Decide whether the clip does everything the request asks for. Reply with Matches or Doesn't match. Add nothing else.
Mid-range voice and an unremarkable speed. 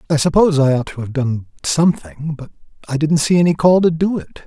Doesn't match